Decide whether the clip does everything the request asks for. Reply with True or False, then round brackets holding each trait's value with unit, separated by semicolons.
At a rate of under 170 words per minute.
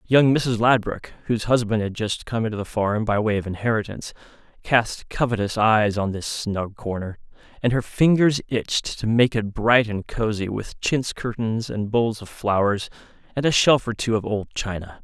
False (190 wpm)